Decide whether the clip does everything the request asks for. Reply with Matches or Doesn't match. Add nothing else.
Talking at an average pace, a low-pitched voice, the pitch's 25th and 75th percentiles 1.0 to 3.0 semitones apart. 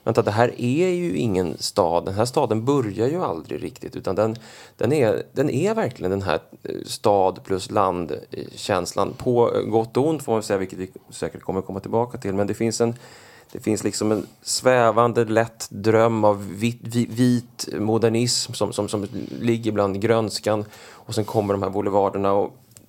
Matches